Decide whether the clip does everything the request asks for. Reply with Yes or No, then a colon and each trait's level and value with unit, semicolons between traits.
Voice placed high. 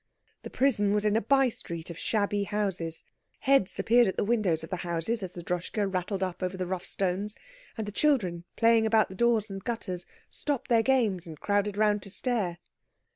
Yes: high, 205 Hz